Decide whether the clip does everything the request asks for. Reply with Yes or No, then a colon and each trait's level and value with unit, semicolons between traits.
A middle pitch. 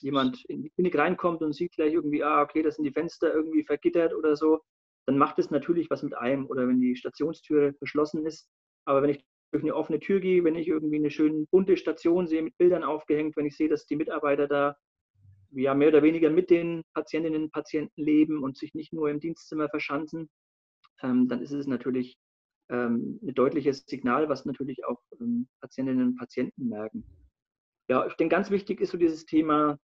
Yes: medium, 150 Hz